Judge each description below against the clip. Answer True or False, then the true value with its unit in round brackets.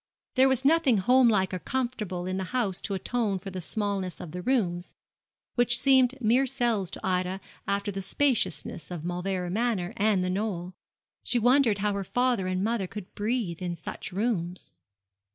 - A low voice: False (200 Hz)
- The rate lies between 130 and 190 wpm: True (175 wpm)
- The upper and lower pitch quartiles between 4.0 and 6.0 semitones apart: True (4.8 semitones)